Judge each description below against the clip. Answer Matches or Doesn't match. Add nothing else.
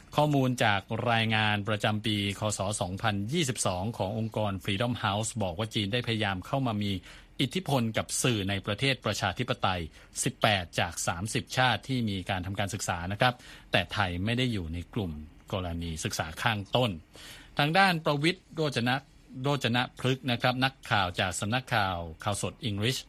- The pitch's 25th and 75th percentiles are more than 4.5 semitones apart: Doesn't match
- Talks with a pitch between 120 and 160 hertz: Doesn't match